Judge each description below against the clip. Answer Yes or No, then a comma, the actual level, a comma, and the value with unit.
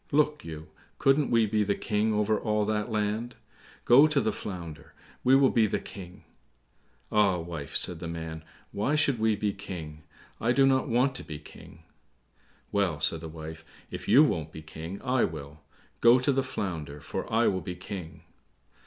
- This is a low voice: Yes, low, 100 Hz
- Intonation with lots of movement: Yes, wide, 6.7 semitones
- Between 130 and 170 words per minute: No, average, 180 wpm